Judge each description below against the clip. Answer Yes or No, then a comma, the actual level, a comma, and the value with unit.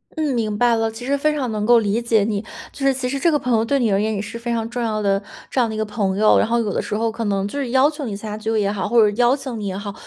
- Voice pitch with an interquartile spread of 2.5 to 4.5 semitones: Yes, average, 3.1 semitones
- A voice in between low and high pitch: No, high, 225 Hz